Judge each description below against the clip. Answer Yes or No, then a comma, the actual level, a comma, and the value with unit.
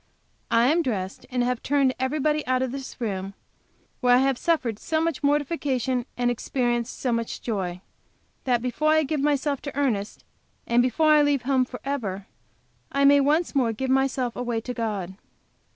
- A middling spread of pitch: Yes, average, 3.2 semitones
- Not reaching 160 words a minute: No, average, 170 wpm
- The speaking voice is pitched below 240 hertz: No, very high, 255 Hz